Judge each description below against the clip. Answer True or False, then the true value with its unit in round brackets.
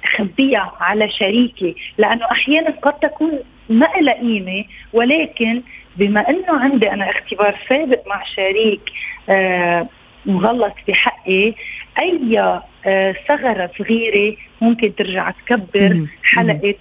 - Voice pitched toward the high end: True (215 Hz)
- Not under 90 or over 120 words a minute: True (95 wpm)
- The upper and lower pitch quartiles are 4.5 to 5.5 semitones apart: False (3.6 semitones)